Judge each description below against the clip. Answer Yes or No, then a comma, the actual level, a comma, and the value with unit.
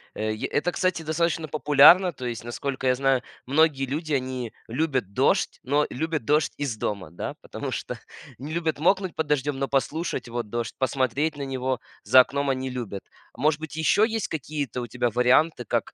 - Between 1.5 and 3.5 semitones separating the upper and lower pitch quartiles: No, average, 3.9 semitones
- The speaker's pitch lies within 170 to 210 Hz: No, low, 135 Hz